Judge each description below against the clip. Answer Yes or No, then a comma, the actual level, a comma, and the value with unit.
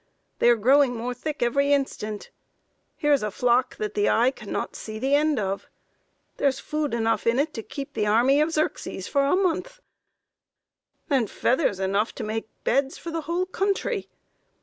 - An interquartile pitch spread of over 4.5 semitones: Yes, average, 5.0 semitones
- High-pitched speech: Yes, very high, 265 Hz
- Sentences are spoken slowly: No, average, 180 wpm